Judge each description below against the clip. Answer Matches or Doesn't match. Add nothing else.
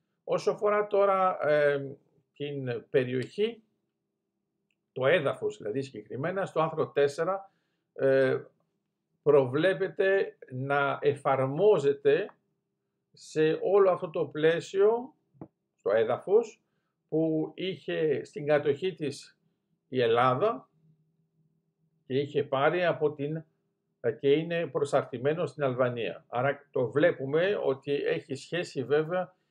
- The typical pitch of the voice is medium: Matches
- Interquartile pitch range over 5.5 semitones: Doesn't match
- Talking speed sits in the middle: Doesn't match